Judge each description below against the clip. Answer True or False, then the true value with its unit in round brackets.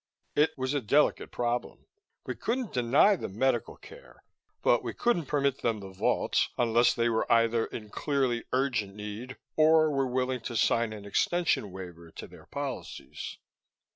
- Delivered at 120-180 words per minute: True (160 wpm)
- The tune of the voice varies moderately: True (4.1 semitones)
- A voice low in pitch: True (120 Hz)